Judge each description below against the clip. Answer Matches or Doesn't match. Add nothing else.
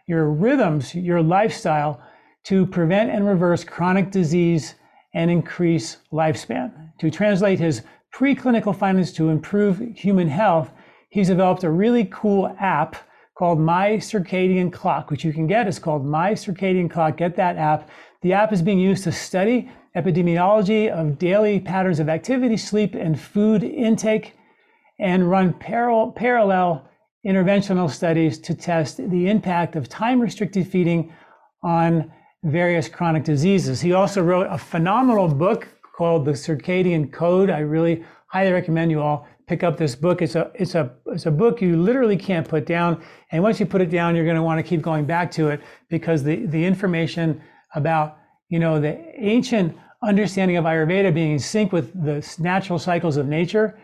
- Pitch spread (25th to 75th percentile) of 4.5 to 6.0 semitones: Doesn't match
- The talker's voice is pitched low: Doesn't match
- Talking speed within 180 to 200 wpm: Doesn't match